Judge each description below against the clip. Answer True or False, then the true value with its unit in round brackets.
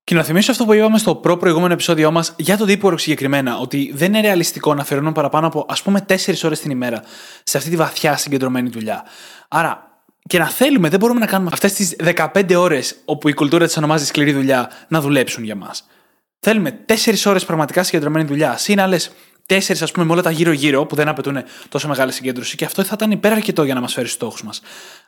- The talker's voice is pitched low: False (165 Hz)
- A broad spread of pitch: False (4.9 semitones)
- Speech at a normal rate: False (220 wpm)